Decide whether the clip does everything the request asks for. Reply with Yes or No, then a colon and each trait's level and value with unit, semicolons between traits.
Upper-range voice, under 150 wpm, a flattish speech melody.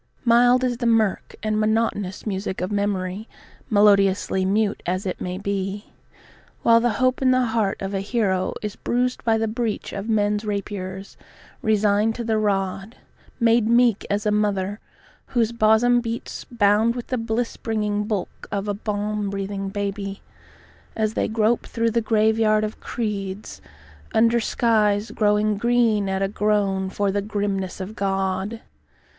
No: high, 210 Hz; average, 155 wpm; narrow, 2.3 semitones